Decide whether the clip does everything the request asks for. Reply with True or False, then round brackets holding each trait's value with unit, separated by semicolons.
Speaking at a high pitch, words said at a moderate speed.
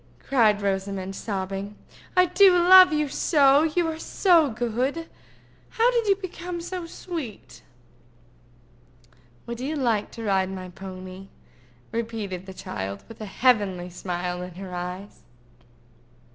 False (220 Hz; 130 wpm)